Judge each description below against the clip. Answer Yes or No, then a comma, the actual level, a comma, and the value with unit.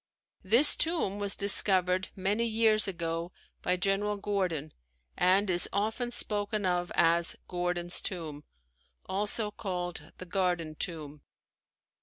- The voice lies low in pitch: No, medium, 185 Hz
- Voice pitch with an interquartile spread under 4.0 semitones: Yes, average, 2.9 semitones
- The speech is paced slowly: Yes, slow, 115 wpm